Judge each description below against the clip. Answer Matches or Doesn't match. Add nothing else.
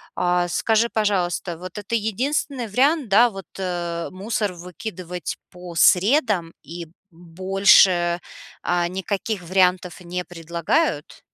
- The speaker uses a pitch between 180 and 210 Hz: Matches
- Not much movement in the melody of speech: Doesn't match